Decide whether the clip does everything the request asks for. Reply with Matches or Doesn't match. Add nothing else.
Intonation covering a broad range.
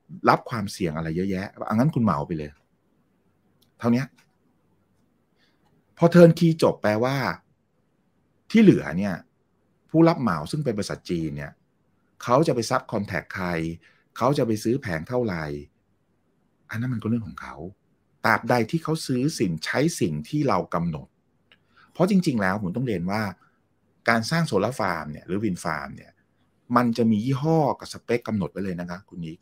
Matches